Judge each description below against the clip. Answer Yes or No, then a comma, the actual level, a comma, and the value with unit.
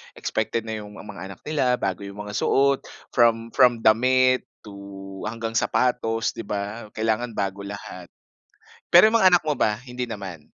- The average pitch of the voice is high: No, low, 115 Hz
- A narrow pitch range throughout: No, average, 3.8 semitones